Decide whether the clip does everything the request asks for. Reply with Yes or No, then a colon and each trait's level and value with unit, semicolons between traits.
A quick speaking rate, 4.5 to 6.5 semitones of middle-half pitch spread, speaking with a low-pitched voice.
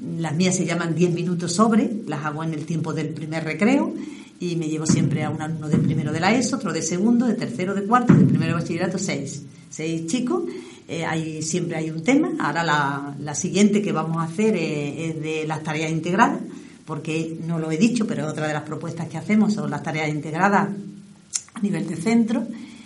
No: fast, 215 wpm; average, 5.2 semitones; medium, 170 Hz